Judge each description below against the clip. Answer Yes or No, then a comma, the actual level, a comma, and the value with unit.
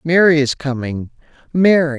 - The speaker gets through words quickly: No, slow, 120 wpm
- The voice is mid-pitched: Yes, medium, 150 Hz